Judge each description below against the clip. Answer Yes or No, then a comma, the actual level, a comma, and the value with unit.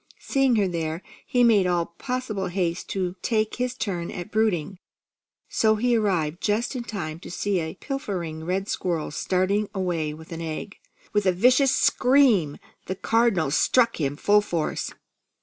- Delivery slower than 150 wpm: No, average, 160 wpm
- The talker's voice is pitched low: No, high, 190 Hz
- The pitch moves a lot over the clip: No, average, 4.9 semitones